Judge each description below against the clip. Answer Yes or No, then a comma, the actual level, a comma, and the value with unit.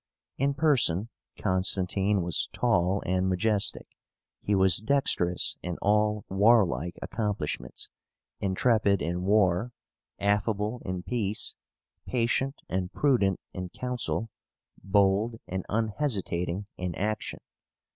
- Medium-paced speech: No, slow, 100 wpm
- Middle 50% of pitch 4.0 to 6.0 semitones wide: No, average, 3.4 semitones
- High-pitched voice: No, low, 100 Hz